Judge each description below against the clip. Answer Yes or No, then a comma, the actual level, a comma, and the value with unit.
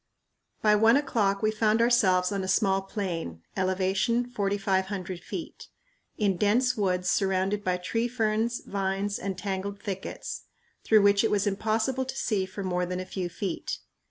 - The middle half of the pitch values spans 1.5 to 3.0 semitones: Yes, narrow, 2.5 semitones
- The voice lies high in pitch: Yes, high, 200 Hz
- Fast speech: No, average, 155 wpm